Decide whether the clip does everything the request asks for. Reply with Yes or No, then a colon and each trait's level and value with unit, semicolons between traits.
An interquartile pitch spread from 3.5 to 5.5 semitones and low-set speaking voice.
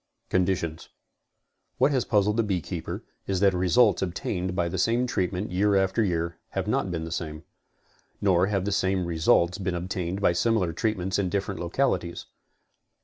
No: average, 2.7 semitones; very low, 95 Hz